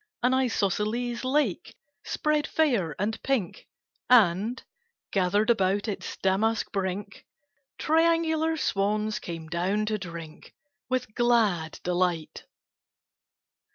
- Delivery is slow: Yes, slow, 95 wpm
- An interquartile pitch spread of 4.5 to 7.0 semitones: Yes, average, 5.1 semitones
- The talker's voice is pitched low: No, high, 210 Hz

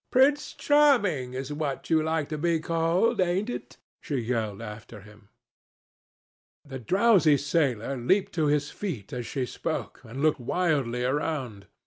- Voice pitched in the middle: Yes, medium, 145 Hz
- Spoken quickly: No, average, 145 wpm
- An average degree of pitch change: No, wide, 5.9 semitones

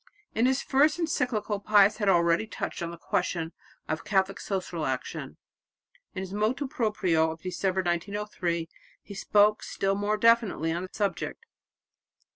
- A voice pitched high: Yes, high, 195 Hz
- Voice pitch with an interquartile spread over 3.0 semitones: Yes, average, 3.6 semitones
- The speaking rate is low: No, average, 145 wpm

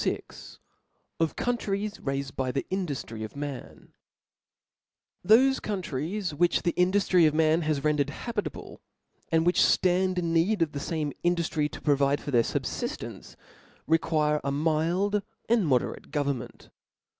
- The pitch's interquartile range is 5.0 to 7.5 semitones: No, average, 4.2 semitones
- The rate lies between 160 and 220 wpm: No, average, 145 wpm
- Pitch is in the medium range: Yes, medium, 160 Hz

